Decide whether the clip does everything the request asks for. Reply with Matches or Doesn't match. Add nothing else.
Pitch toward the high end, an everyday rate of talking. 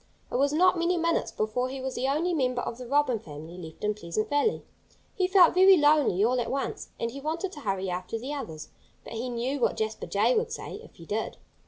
Doesn't match